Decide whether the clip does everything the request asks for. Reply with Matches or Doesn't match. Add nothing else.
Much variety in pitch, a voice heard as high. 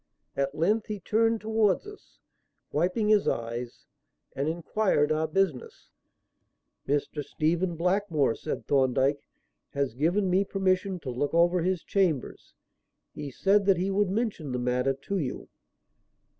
Doesn't match